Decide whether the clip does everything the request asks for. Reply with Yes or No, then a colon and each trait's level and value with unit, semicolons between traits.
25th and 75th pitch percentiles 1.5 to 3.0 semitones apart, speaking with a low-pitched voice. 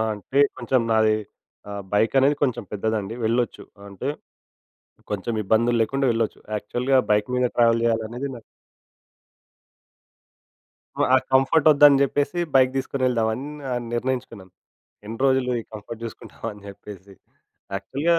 No: average, 3.6 semitones; low, 115 Hz